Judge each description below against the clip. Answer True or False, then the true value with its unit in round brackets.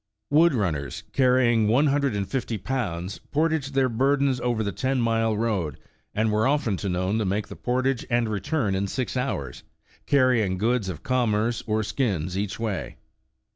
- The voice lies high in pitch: False (115 Hz)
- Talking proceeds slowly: False (170 wpm)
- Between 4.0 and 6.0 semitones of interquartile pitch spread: True (4.5 semitones)